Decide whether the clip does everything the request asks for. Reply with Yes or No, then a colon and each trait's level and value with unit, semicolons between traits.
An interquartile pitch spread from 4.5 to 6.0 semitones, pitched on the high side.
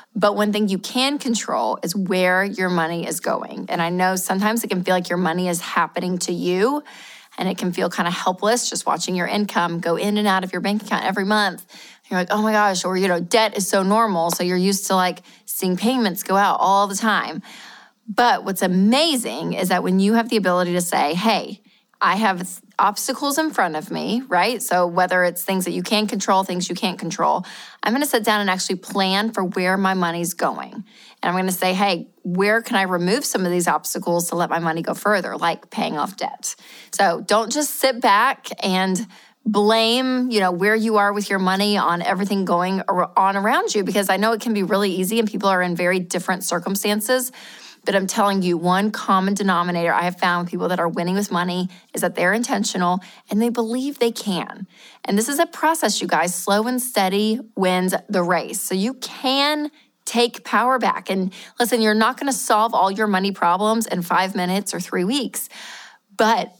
No: average, 3.4 semitones; high, 195 Hz